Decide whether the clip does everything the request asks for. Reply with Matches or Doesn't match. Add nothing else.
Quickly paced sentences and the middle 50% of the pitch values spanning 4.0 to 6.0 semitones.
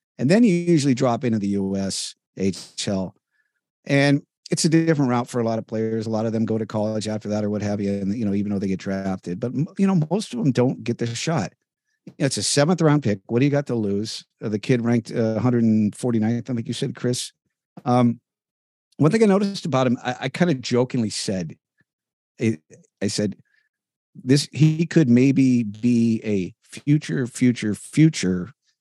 Matches